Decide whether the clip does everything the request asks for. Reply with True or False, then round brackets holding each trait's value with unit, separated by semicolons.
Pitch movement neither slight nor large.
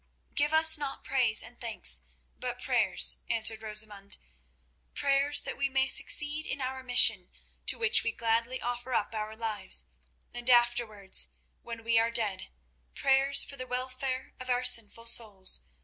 True (3.2 semitones)